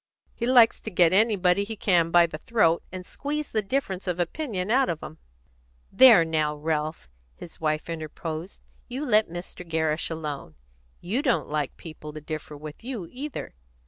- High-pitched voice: No, medium, 175 Hz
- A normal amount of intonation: No, wide, 5.9 semitones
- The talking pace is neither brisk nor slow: Yes, average, 170 wpm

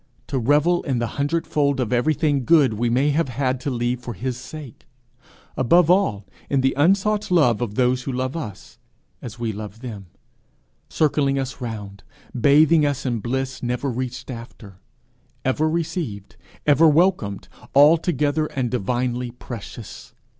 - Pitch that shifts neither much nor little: Yes, average, 3.9 semitones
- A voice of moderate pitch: No, low, 130 Hz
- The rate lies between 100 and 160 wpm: Yes, average, 145 wpm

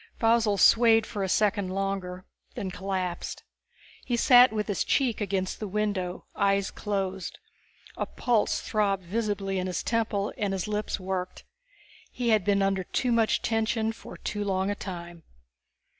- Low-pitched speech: No, high, 200 Hz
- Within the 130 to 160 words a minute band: Yes, average, 155 wpm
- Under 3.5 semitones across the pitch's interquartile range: Yes, narrow, 2.6 semitones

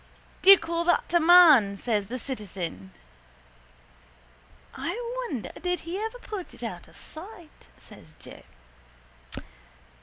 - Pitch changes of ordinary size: No, wide, 8.0 semitones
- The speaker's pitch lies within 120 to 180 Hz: No, very high, 335 Hz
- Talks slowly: Yes, slow, 125 wpm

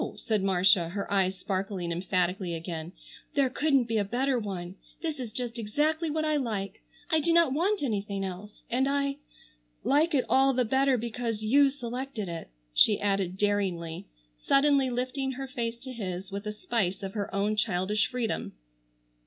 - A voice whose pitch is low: No, high, 220 Hz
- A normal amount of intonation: No, wide, 5.7 semitones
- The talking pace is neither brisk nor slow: Yes, average, 165 wpm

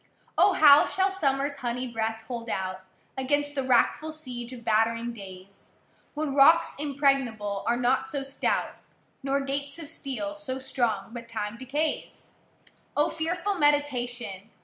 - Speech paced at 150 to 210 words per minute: No, average, 140 wpm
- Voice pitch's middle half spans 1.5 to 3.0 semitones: No, average, 3.9 semitones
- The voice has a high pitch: Yes, very high, 265 Hz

